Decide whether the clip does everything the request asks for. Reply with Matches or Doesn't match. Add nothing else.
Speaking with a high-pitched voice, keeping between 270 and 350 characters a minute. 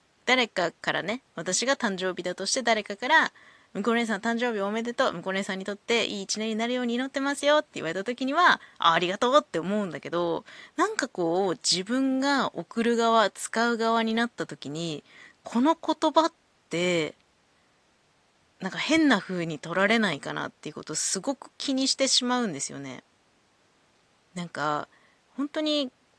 Matches